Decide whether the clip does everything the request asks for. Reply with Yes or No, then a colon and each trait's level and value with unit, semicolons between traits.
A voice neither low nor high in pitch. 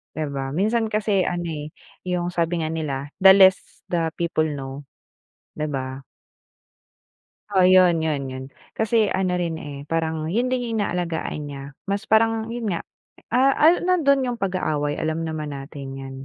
Yes: medium, 170 Hz